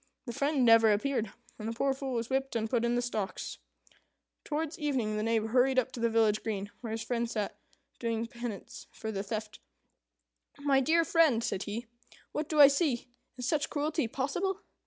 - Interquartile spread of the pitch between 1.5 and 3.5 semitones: No, average, 3.9 semitones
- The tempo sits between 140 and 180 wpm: No, average, 190 wpm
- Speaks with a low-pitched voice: No, high, 240 Hz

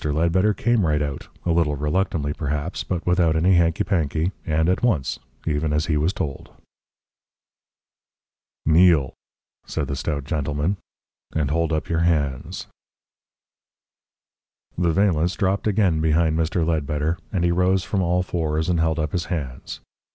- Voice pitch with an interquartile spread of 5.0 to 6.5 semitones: No, average, 2.9 semitones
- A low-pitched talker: Yes, very low, 80 Hz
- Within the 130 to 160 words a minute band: Yes, average, 145 wpm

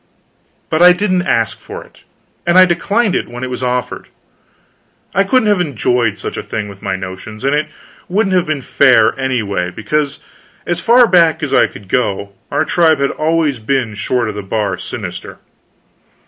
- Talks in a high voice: No, medium, 140 Hz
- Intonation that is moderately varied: No, wide, 8.2 semitones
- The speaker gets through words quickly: No, average, 180 wpm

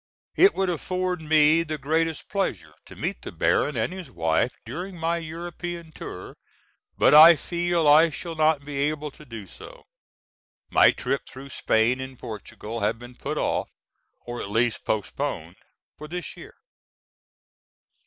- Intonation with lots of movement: Yes, wide, 5.8 semitones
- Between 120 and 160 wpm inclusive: Yes, average, 155 wpm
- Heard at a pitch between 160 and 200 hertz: No, medium, 150 Hz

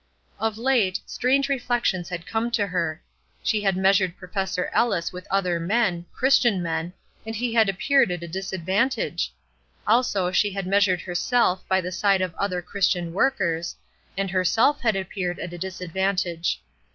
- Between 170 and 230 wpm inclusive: No, average, 155 wpm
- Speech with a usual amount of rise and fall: Yes, average, 3.8 semitones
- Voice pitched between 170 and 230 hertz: Yes, high, 190 Hz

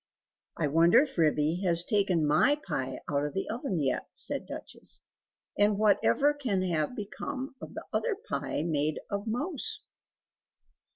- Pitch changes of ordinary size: No, wide, 8.9 semitones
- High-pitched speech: Yes, high, 195 Hz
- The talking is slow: No, average, 150 wpm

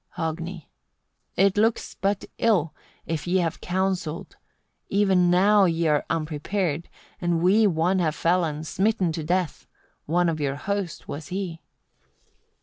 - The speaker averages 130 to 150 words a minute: Yes, average, 145 wpm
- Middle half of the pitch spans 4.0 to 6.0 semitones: No, average, 3.0 semitones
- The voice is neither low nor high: Yes, medium, 175 Hz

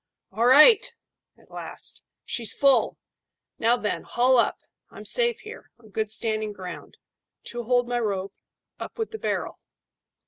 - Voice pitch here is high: Yes, high, 240 Hz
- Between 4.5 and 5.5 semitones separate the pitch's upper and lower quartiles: No, average, 3.8 semitones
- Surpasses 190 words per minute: No, average, 145 wpm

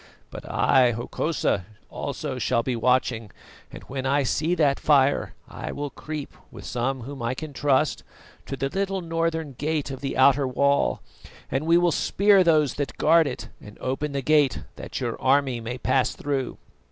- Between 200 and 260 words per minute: No, average, 175 wpm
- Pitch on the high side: No, medium, 140 Hz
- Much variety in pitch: No, average, 3.1 semitones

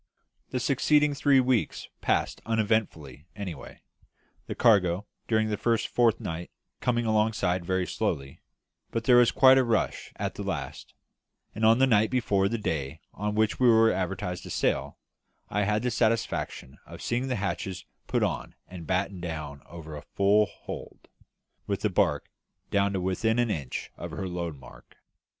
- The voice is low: Yes, low, 105 Hz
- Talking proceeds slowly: No, average, 165 wpm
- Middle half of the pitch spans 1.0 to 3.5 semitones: No, average, 4.5 semitones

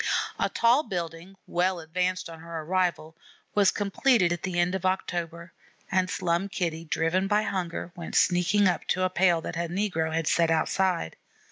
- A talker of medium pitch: Yes, medium, 180 Hz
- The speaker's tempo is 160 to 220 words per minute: Yes, average, 170 wpm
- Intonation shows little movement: Yes, narrow, 2.2 semitones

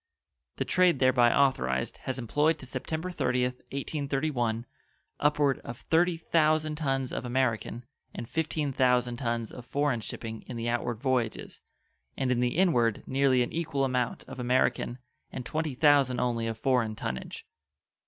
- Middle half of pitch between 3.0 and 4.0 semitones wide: Yes, average, 3.5 semitones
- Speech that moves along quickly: No, average, 150 wpm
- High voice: No, low, 130 Hz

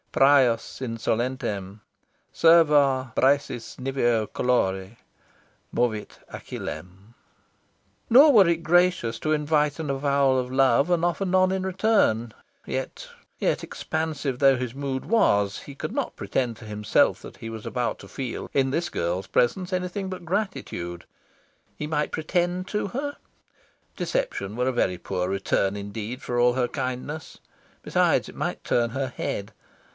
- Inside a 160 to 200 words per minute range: No, average, 140 wpm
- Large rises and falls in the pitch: Yes, wide, 6.3 semitones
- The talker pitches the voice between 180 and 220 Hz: No, low, 130 Hz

